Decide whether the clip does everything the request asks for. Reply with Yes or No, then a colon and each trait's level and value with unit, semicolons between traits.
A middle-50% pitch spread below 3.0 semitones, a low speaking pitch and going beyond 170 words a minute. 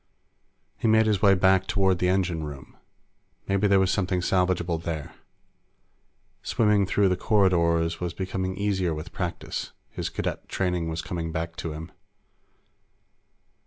No: narrow, 2.6 semitones; very low, 90 Hz; average, 140 wpm